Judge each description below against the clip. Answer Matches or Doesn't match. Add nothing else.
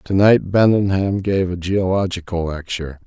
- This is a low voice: Matches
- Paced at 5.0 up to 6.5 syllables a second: Doesn't match